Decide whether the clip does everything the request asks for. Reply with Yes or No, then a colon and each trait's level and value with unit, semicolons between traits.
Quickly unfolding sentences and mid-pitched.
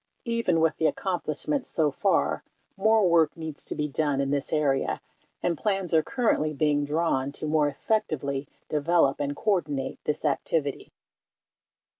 No: average, 145 wpm; medium, 155 Hz